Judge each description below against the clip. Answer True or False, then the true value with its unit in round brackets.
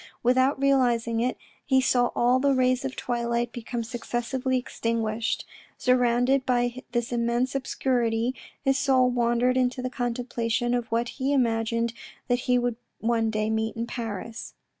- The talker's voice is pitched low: False (245 Hz)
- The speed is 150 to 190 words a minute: True (155 wpm)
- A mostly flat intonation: True (1.6 semitones)